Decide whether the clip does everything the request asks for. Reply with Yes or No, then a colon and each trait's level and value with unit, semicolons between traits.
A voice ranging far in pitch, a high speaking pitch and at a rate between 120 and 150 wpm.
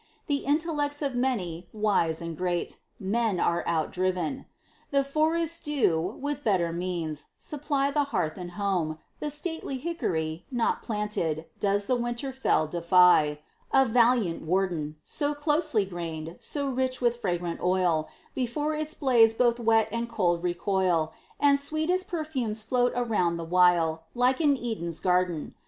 Yes: wide, 7.9 semitones; high, 215 Hz; average, 145 wpm